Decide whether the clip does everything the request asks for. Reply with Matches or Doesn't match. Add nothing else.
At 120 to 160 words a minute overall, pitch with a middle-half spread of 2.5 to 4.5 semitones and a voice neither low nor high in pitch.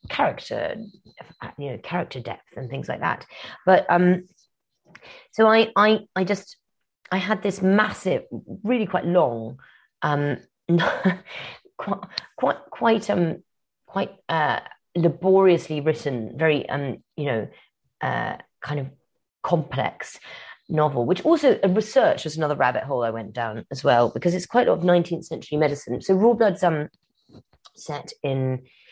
Doesn't match